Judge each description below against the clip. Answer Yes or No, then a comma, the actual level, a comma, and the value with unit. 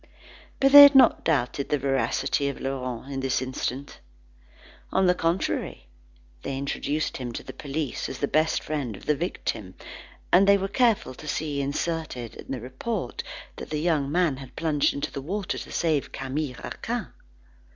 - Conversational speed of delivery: Yes, average, 170 wpm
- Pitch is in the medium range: Yes, medium, 145 Hz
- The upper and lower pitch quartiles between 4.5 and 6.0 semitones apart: No, average, 3.8 semitones